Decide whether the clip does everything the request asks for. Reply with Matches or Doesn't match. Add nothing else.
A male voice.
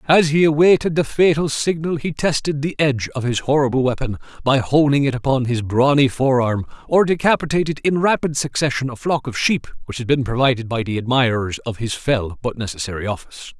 Matches